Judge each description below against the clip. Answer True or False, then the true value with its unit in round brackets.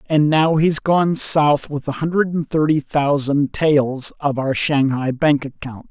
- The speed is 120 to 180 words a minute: True (175 wpm)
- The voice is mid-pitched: True (145 Hz)